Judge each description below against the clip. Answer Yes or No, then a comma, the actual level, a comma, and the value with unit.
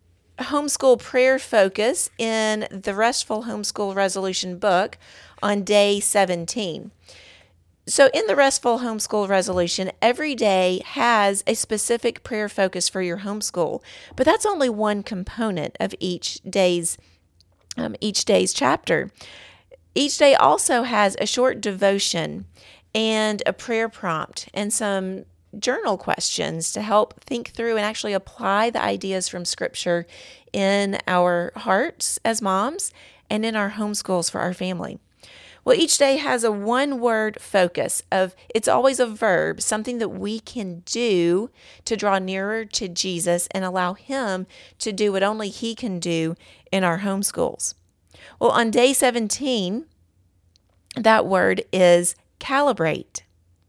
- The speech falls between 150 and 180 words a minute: No, slow, 135 wpm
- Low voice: No, high, 205 Hz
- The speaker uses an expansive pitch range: No, average, 4.0 semitones